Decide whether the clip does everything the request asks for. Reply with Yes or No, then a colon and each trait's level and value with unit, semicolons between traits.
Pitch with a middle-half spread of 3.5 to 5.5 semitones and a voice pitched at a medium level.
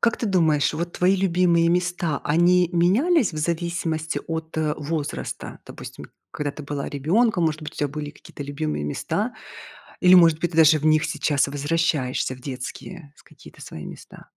No: average, 2.9 semitones; medium, 160 Hz